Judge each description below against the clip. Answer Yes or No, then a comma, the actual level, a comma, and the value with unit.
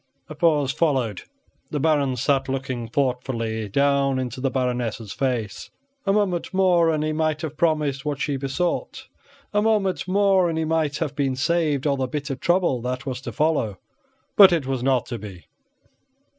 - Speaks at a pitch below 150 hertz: Yes, medium, 140 Hz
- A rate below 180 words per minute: Yes, average, 170 wpm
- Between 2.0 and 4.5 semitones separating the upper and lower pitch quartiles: Yes, average, 4.0 semitones